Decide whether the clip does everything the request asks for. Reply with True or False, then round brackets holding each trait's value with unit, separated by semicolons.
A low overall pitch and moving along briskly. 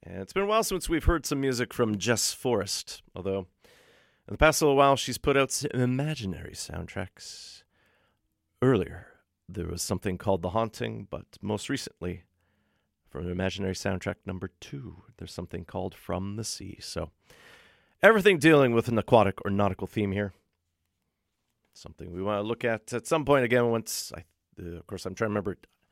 False (100 Hz; 180 wpm)